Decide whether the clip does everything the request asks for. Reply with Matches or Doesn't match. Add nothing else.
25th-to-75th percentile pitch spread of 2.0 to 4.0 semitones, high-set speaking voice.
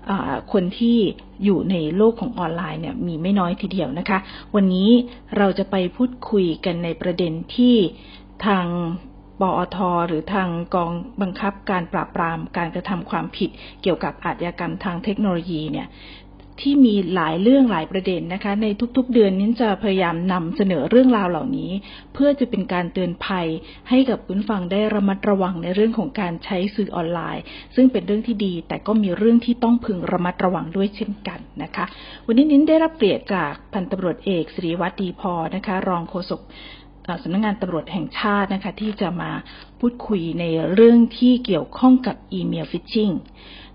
Matches